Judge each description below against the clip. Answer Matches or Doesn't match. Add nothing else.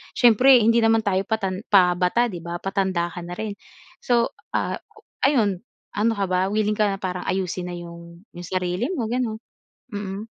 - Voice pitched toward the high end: Matches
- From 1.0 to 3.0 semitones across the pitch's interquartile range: Doesn't match